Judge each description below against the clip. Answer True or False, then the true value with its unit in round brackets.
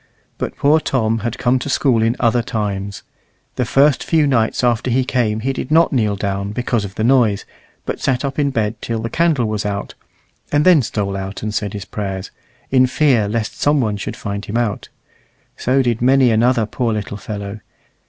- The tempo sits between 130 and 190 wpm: False (200 wpm)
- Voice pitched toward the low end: True (115 Hz)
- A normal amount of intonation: True (3.8 semitones)